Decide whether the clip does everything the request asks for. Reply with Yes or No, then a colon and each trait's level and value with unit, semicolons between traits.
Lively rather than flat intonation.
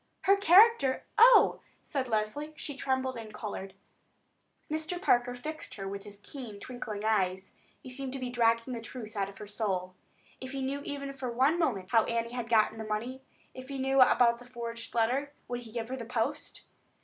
No: average, 3.5 semitones